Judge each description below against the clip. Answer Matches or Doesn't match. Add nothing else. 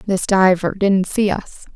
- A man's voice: Doesn't match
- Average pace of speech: Matches